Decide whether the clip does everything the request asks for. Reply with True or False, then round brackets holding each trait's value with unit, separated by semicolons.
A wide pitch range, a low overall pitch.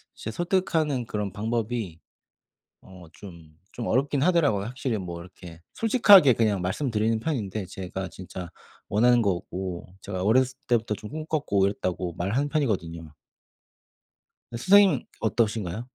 True (5.9 semitones; 110 Hz)